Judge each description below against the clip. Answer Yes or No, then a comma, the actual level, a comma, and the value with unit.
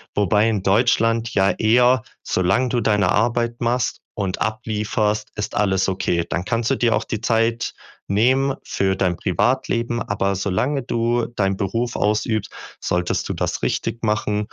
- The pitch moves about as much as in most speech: Yes, average, 3.1 semitones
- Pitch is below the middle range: Yes, low, 110 Hz